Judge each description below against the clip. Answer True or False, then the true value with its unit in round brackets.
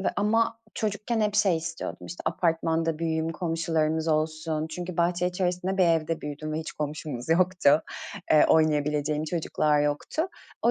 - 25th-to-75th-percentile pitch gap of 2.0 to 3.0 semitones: True (2.7 semitones)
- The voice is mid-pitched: True (160 Hz)